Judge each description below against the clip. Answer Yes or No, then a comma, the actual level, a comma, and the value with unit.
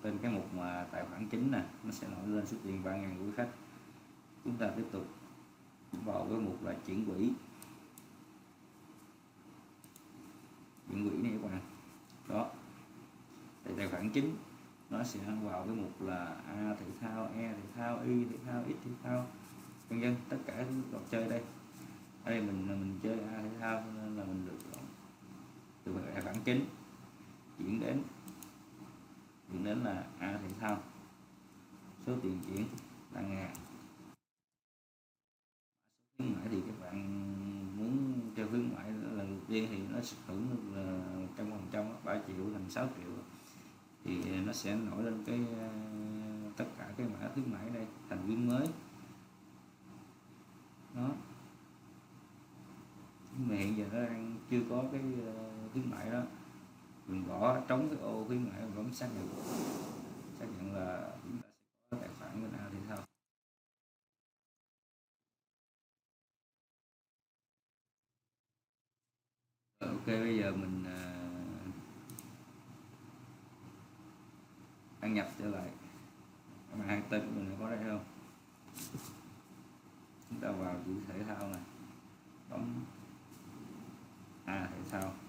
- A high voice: No, low, 100 Hz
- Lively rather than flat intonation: Yes, wide, 6.0 semitones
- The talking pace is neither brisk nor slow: No, slow, 140 wpm